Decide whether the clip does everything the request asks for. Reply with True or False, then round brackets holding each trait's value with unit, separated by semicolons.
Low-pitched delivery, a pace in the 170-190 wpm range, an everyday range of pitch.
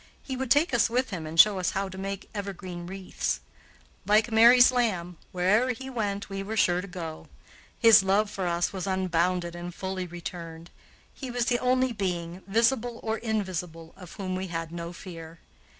False (195 Hz; 180 wpm; 4.3 semitones)